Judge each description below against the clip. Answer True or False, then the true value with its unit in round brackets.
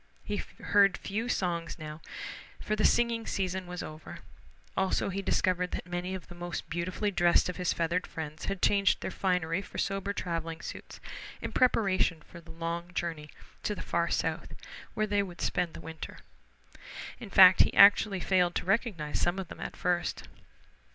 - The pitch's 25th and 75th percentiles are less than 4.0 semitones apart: True (2.6 semitones)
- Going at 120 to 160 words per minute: False (175 wpm)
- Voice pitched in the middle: True (180 Hz)